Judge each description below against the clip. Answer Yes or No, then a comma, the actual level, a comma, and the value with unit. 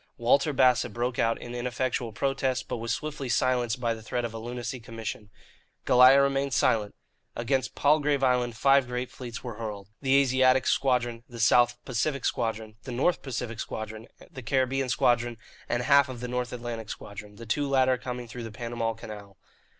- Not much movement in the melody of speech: Yes, narrow, 2.3 semitones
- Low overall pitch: Yes, low, 120 Hz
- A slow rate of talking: No, average, 175 wpm